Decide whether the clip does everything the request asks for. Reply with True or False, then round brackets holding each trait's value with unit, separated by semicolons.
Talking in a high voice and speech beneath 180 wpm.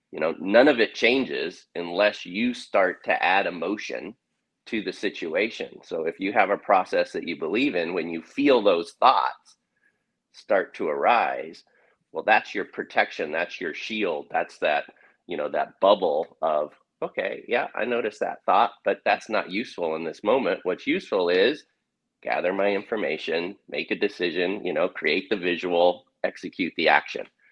True (400 Hz; 170 wpm)